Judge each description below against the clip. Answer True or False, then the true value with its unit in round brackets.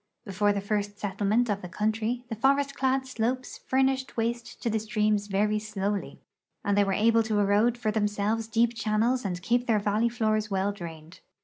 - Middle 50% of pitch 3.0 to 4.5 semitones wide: False (2.5 semitones)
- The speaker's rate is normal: True (185 wpm)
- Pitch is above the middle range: True (215 Hz)